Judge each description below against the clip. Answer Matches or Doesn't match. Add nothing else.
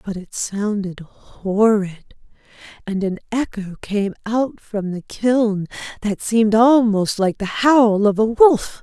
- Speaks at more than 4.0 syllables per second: Doesn't match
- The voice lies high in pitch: Matches